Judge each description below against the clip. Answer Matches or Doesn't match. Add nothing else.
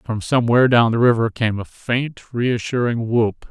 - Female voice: Doesn't match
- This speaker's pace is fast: Doesn't match